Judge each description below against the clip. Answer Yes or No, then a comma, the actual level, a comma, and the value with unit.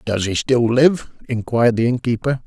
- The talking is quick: No, average, 170 wpm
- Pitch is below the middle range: Yes, low, 120 Hz